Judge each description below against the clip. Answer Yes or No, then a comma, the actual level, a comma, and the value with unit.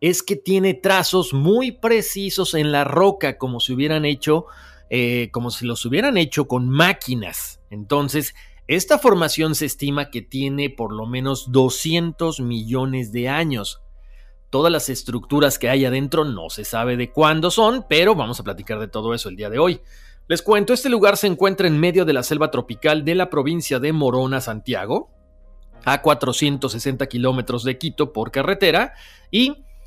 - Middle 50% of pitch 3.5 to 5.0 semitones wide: No, wide, 5.4 semitones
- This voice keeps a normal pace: Yes, average, 170 wpm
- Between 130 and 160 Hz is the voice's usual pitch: Yes, medium, 140 Hz